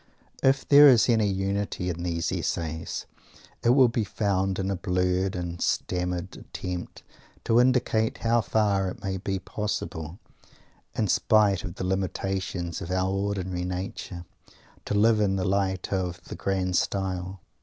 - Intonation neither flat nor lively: No, narrow, 2.3 semitones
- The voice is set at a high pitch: No, very low, 95 Hz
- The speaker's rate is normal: Yes, average, 150 wpm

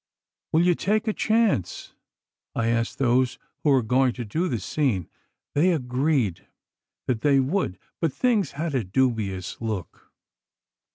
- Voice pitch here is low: Yes, low, 130 Hz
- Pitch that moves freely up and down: Yes, wide, 6.1 semitones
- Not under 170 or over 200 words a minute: No, average, 145 wpm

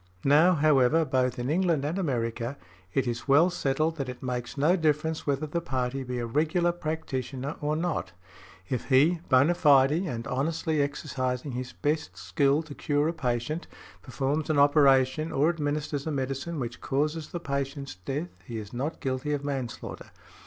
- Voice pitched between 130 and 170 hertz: Yes, medium, 140 Hz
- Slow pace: No, average, 165 wpm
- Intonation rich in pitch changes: No, average, 3.4 semitones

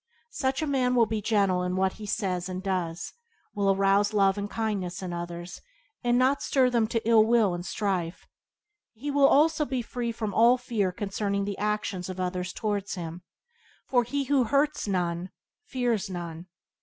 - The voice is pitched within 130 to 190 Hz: No, high, 205 Hz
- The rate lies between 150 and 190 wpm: Yes, average, 180 wpm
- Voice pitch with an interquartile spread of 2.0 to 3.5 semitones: No, average, 4.7 semitones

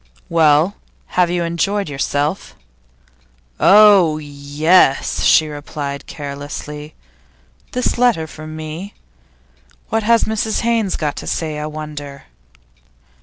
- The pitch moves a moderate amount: Yes, average, 5.0 semitones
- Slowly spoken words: Yes, slow, 105 wpm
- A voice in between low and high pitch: Yes, medium, 155 Hz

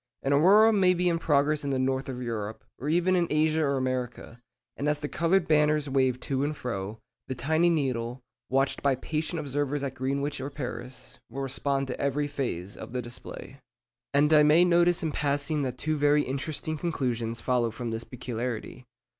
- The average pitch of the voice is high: No, medium, 140 Hz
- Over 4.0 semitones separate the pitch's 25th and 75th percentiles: No, average, 3.3 semitones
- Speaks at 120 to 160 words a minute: No, average, 190 wpm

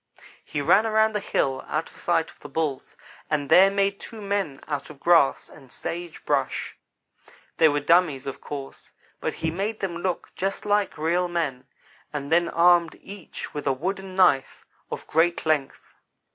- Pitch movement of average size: Yes, average, 4.8 semitones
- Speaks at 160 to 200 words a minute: Yes, average, 175 wpm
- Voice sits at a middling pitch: Yes, medium, 170 Hz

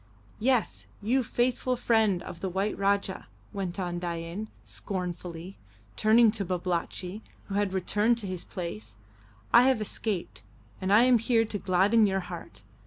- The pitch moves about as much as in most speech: Yes, average, 3.7 semitones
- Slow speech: No, average, 150 wpm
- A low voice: No, high, 195 Hz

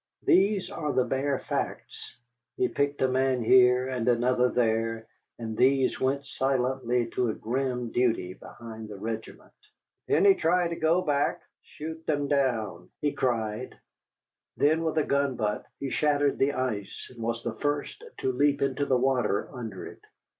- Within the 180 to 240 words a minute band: No, average, 160 wpm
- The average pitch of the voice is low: Yes, low, 130 Hz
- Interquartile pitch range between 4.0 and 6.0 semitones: No, average, 3.5 semitones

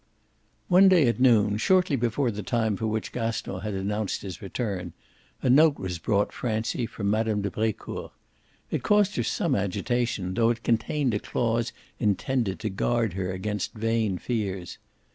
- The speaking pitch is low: Yes, low, 110 Hz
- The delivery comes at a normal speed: Yes, average, 165 wpm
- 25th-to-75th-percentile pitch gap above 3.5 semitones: No, average, 3.2 semitones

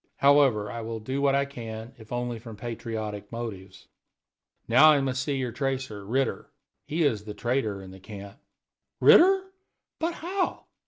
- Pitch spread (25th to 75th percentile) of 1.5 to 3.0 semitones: No, average, 4.4 semitones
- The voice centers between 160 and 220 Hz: No, low, 120 Hz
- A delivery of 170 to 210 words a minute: No, average, 160 wpm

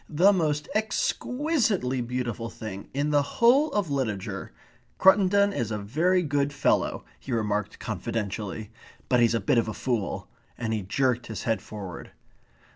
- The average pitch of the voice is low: Yes, low, 125 Hz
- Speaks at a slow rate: No, average, 160 wpm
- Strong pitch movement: Yes, wide, 8.5 semitones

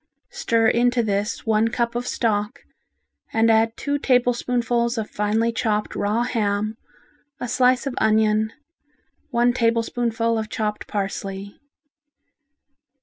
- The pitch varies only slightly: Yes, narrow, 2.1 semitones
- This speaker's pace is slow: Yes, slow, 115 wpm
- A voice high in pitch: Yes, high, 230 Hz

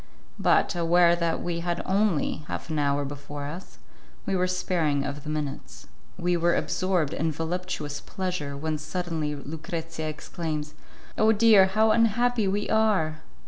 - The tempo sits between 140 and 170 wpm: Yes, average, 145 wpm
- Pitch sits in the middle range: Yes, medium, 170 Hz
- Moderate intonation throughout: Yes, average, 3.6 semitones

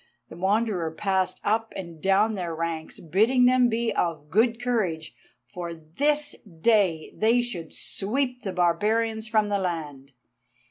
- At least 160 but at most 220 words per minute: No, average, 140 wpm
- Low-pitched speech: No, high, 195 Hz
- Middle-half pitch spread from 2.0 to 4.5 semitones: No, average, 5.3 semitones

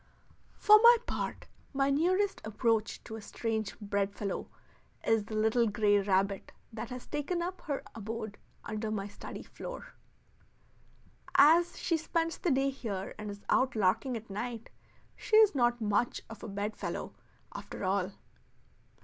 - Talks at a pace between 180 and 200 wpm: No, average, 145 wpm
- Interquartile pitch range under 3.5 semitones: No, average, 5.3 semitones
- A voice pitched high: Yes, high, 225 Hz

